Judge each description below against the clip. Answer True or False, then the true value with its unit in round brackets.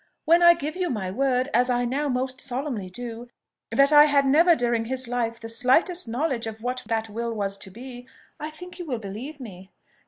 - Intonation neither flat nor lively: True (4.2 semitones)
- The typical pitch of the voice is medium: False (250 Hz)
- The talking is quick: True (210 wpm)